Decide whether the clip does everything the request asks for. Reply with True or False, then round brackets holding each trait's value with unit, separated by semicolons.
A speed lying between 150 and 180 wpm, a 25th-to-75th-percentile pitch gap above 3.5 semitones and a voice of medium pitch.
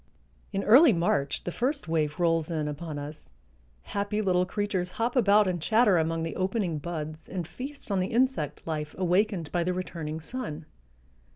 True (170 wpm; 4.7 semitones; 180 Hz)